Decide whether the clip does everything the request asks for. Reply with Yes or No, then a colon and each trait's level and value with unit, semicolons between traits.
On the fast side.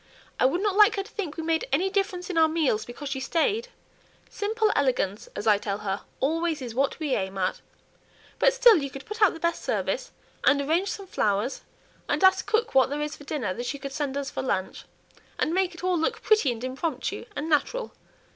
Yes: fast, 220 wpm